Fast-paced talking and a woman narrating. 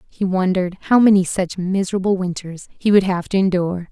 No: average, 185 wpm; female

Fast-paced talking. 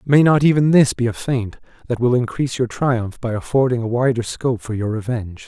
Yes: fast, 220 wpm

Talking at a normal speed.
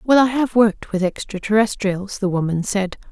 Yes: average, 175 wpm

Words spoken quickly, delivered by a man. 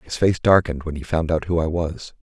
Yes: fast, 265 wpm; male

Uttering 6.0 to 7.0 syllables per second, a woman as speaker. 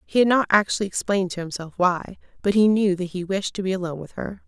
Yes: 6.5 syllables/s; female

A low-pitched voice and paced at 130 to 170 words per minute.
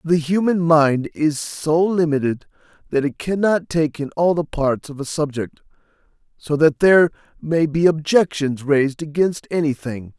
No: medium, 155 Hz; average, 160 wpm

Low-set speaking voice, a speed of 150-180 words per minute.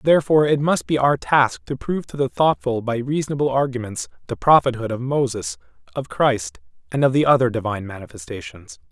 Yes: low, 130 Hz; average, 175 wpm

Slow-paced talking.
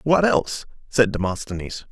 Yes: slow, 125 wpm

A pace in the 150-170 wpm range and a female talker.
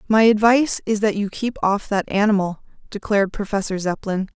Yes: average, 165 wpm; female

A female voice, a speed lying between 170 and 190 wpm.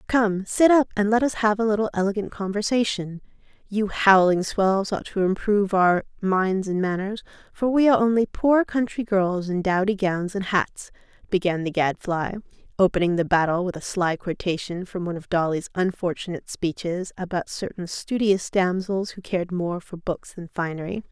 Yes: female; average, 175 wpm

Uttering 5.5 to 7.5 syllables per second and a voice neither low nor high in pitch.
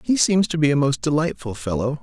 Yes: 5.7 syllables/s; medium, 145 Hz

